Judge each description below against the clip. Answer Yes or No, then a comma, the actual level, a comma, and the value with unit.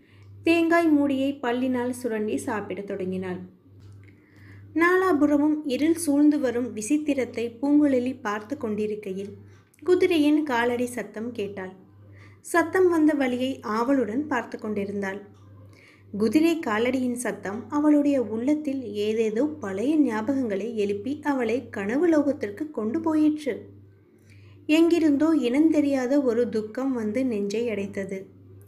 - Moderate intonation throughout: No, wide, 6.4 semitones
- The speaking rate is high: No, average, 95 wpm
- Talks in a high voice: Yes, high, 240 Hz